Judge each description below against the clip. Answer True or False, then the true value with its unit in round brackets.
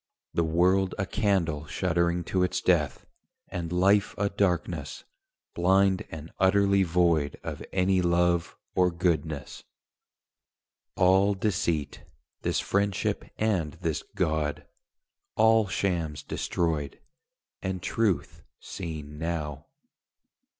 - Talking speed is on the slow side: True (100 wpm)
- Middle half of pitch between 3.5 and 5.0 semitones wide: False (3.0 semitones)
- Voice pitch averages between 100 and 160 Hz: False (90 Hz)